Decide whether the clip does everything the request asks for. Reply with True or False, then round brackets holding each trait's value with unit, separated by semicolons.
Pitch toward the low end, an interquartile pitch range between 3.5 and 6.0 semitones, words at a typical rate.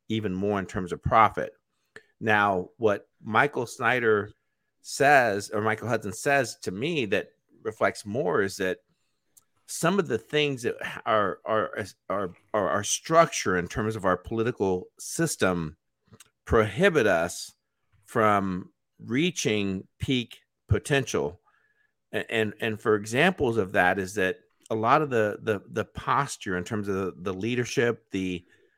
True (110 Hz; 4.7 semitones; 145 wpm)